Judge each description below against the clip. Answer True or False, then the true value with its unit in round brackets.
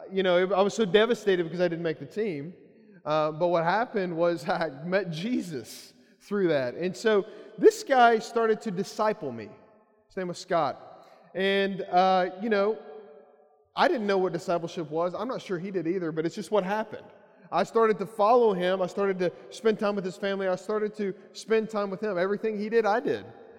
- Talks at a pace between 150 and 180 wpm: False (205 wpm)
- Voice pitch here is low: False (195 Hz)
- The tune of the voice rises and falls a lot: False (3.2 semitones)